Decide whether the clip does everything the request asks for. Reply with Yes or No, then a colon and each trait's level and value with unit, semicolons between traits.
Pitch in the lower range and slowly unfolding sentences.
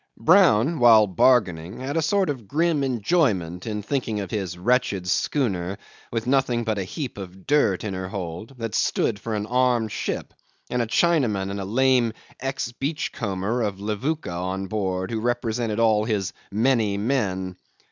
No: low, 110 Hz; average, 165 wpm